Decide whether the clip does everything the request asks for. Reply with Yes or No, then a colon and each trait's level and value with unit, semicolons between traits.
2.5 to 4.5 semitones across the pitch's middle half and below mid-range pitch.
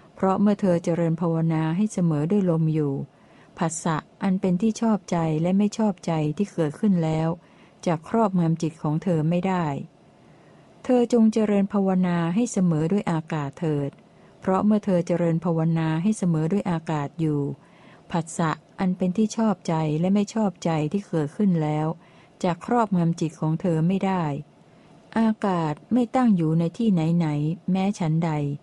No: average, 3.8 semitones; medium, 175 Hz